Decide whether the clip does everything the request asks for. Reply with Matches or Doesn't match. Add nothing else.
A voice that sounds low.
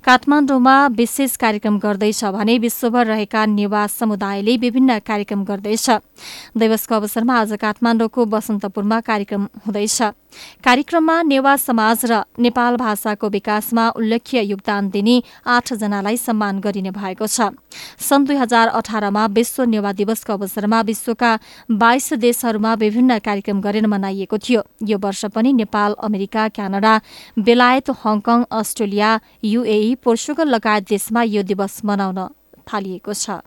Doesn't match